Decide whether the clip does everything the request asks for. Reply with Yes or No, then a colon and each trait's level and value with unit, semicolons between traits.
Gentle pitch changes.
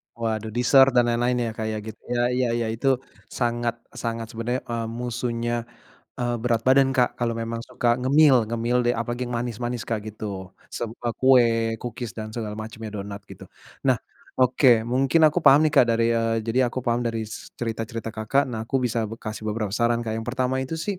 Yes: narrow, 1.7 semitones